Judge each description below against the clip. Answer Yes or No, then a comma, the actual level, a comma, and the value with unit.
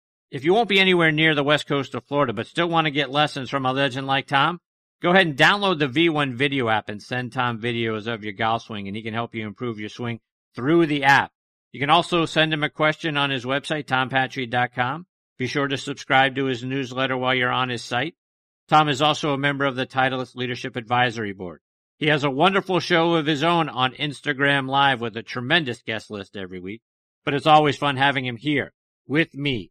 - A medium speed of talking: No, fast, 220 wpm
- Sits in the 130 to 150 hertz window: Yes, low, 135 Hz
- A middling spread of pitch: Yes, average, 3.6 semitones